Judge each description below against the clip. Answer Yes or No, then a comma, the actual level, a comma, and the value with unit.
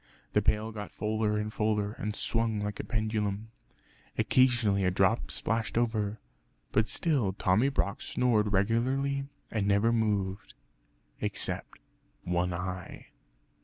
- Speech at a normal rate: No, slow, 125 wpm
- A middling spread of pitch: No, narrow, 2.2 semitones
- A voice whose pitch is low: Yes, low, 105 Hz